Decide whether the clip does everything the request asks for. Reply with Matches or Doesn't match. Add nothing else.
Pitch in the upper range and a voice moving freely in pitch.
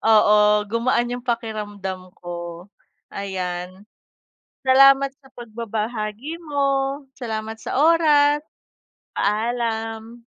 Doesn't match